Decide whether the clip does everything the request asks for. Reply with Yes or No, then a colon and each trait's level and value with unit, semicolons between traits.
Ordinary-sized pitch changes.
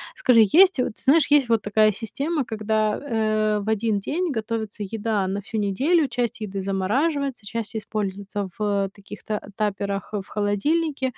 Yes: average, 4.0 semitones